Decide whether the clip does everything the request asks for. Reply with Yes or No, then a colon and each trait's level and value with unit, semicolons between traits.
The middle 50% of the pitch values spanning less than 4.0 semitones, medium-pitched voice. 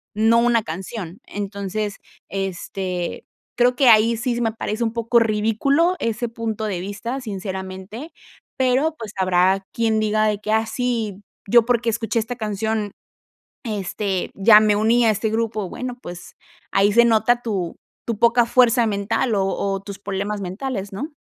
No: average, 2.9 semitones; high, 215 Hz